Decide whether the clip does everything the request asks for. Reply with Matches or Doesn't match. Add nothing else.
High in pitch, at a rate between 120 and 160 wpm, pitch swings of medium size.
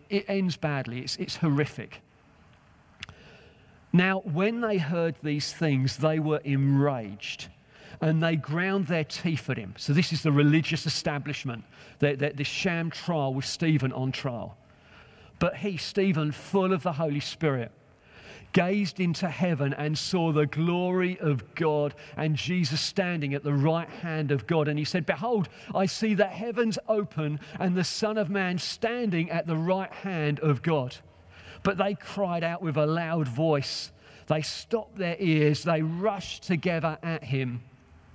Doesn't match